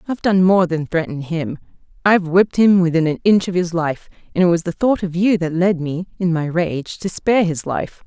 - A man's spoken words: No, female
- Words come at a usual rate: No, fast, 240 wpm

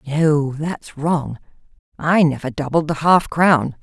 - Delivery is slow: Yes, slow, 125 wpm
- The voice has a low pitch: No, medium, 150 Hz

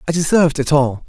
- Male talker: Yes, male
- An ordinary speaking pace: No, fast, 220 wpm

